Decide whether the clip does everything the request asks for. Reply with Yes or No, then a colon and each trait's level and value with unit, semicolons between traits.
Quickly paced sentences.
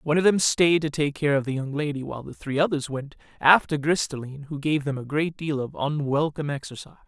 Yes: fast, 245 wpm